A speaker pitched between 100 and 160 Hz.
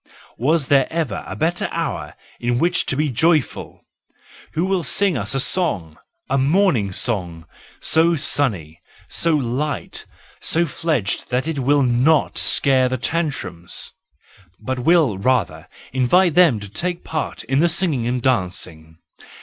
Yes: low, 135 Hz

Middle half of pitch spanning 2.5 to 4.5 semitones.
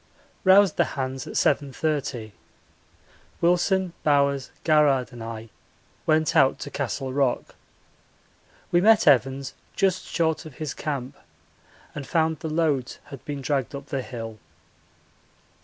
Yes: average, 3.3 semitones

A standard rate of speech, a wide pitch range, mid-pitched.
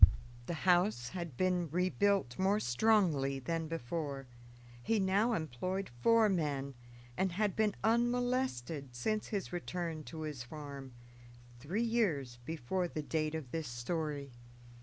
No: slow, 130 wpm; wide, 6.0 semitones; medium, 165 Hz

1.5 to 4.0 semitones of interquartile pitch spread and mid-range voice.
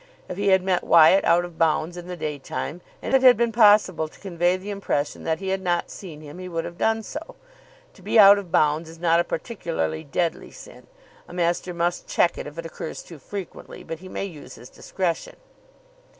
Yes: average, 2.9 semitones; medium, 175 Hz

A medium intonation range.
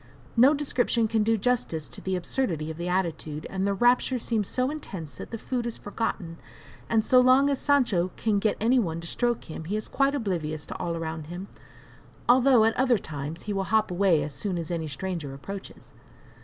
No: wide, 6.5 semitones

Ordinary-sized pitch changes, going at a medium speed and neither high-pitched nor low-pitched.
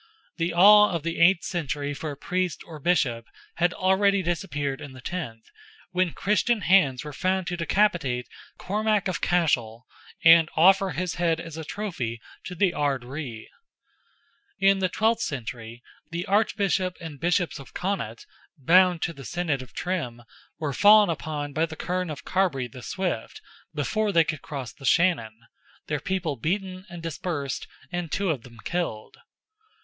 Yes: average, 4.9 semitones; average, 160 wpm; medium, 170 Hz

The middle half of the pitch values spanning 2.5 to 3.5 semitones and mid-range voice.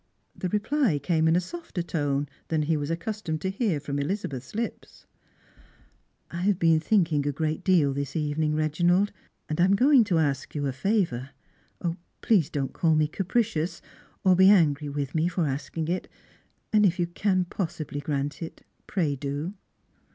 No: average, 4.4 semitones; medium, 160 Hz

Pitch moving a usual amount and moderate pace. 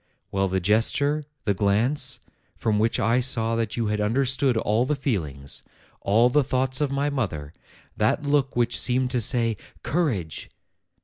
Yes: average, 4.1 semitones; average, 160 wpm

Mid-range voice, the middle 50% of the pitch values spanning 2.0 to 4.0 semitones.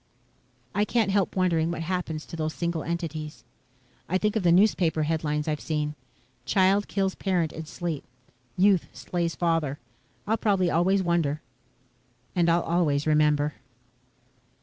Yes: medium, 170 Hz; average, 3.2 semitones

